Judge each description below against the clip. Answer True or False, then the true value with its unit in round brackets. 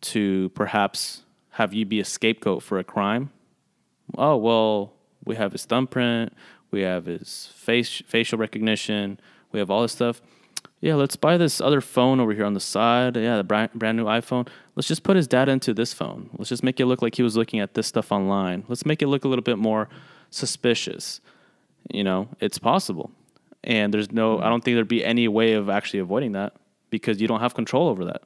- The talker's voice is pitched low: True (115 Hz)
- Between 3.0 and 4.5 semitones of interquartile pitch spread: False (2.6 semitones)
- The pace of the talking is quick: True (210 wpm)